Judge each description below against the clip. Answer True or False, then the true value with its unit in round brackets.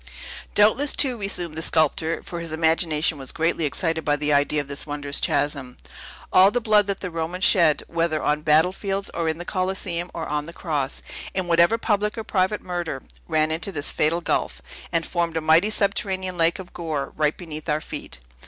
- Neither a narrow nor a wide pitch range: True (3.4 semitones)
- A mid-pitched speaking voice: True (165 Hz)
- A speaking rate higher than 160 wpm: True (190 wpm)